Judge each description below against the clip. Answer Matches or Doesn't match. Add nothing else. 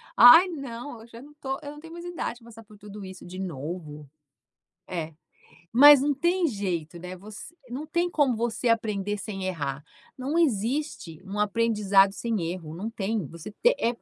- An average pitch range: Doesn't match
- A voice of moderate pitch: Doesn't match